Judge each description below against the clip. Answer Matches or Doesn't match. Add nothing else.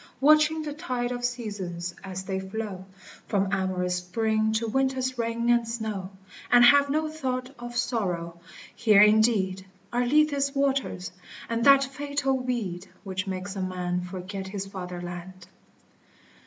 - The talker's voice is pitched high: Matches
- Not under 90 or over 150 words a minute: Matches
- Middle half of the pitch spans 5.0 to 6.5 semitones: Matches